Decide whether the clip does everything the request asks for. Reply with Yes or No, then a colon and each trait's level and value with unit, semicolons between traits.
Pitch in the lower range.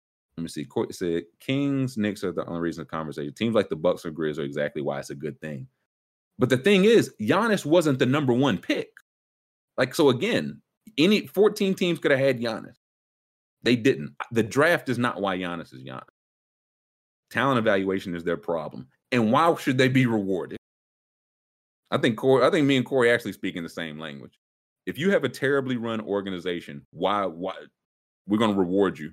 Yes: low, 105 Hz